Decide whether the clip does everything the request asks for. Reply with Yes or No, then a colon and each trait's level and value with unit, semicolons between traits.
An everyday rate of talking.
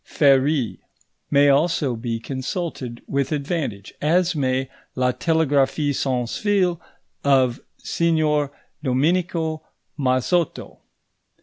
No: slow, 90 wpm